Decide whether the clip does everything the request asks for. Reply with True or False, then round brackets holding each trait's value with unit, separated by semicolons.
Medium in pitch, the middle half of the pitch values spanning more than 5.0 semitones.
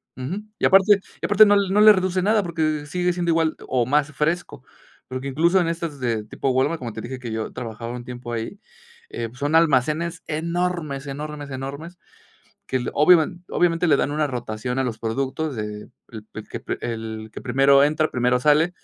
True (145 Hz; 5.4 semitones)